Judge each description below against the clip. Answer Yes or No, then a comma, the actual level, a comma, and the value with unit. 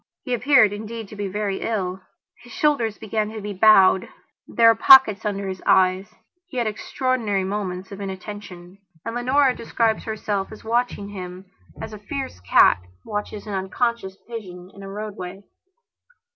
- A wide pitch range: No, average, 3.0 semitones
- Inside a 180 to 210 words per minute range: No, average, 160 wpm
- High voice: Yes, high, 210 Hz